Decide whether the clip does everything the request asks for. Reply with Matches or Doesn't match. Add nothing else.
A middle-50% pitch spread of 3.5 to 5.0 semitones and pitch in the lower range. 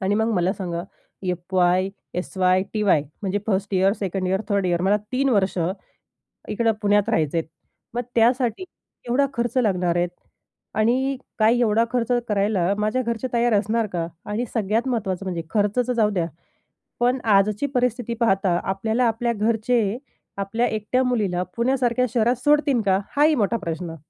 Doesn't match